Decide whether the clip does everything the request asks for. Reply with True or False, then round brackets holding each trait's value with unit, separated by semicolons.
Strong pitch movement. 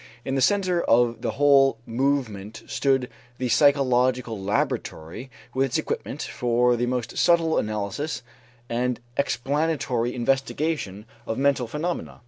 False (3.2 semitones)